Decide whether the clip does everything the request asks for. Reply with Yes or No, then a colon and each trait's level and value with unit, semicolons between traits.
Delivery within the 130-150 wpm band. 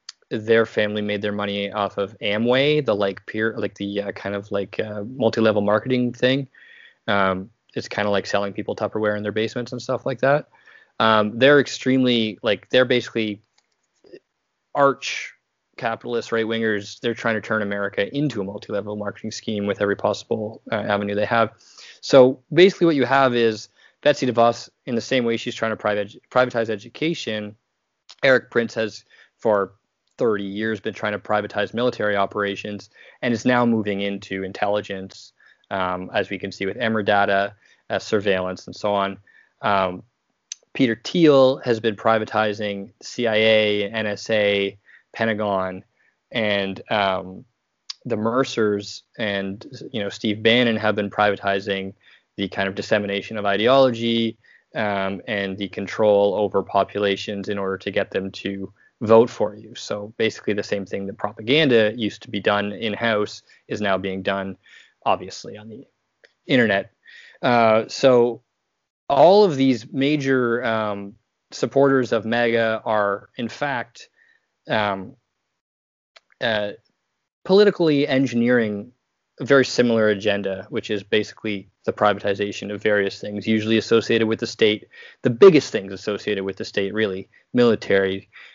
Yes: average, 145 wpm